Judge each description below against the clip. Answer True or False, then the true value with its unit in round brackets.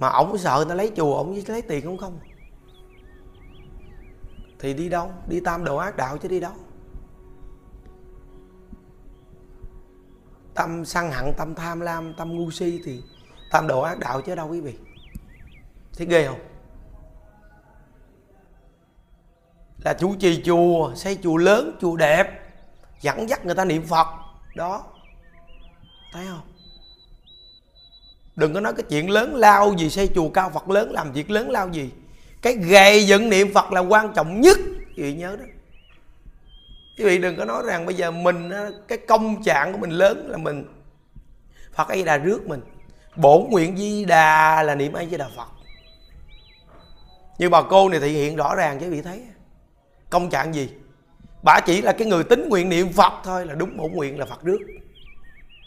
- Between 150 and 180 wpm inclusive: True (170 wpm)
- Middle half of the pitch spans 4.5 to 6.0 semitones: True (5.1 semitones)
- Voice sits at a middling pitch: True (170 Hz)